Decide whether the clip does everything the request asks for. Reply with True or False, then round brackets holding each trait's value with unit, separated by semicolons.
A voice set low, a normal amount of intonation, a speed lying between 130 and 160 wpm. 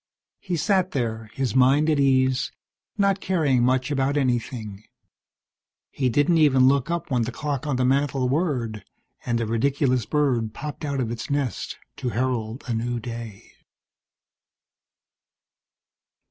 True (130 Hz; 3.4 semitones; 140 wpm)